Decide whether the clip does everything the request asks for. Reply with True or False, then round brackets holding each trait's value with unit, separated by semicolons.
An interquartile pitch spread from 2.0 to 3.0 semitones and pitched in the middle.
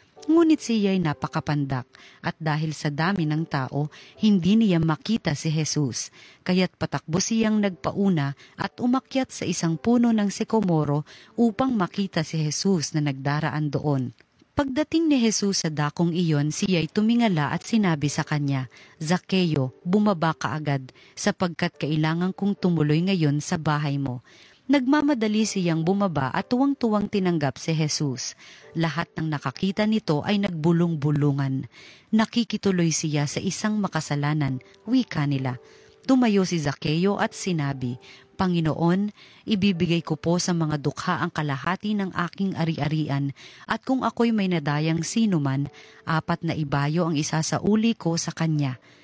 False (5.2 semitones; 165 Hz)